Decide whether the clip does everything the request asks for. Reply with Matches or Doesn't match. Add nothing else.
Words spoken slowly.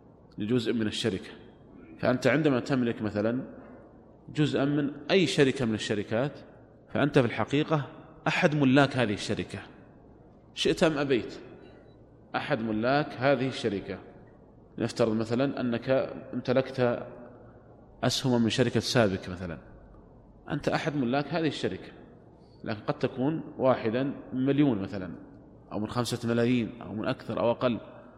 Doesn't match